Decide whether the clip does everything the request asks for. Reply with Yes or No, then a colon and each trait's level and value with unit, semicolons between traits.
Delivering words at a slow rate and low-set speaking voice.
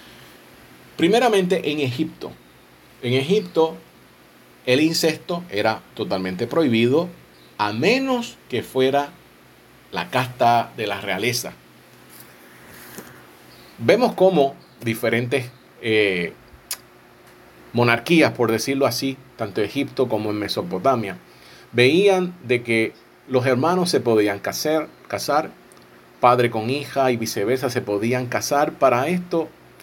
Yes: slow, 105 wpm; low, 125 Hz